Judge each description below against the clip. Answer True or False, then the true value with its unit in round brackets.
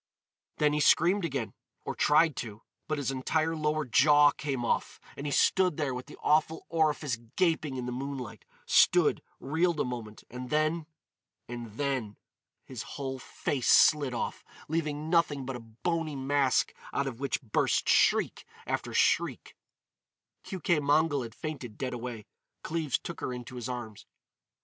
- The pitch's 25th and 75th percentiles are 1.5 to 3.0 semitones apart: False (3.7 semitones)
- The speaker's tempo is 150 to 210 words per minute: False (140 wpm)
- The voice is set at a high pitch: False (140 Hz)